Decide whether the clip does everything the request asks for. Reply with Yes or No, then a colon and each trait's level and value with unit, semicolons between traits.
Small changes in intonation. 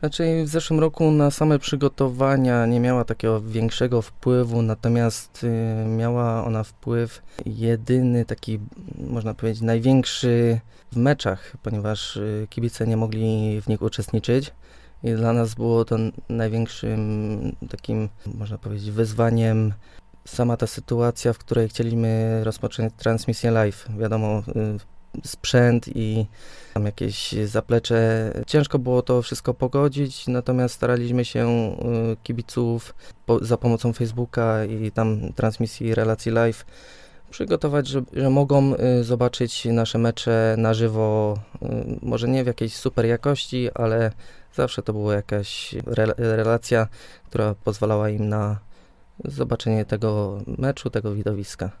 Yes: narrow, 2.1 semitones